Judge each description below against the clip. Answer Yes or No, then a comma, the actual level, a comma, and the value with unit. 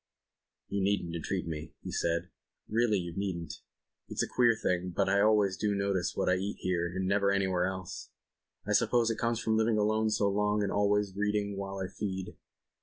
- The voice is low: Yes, low, 100 Hz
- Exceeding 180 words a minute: Yes, average, 195 wpm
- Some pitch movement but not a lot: No, narrow, 2.1 semitones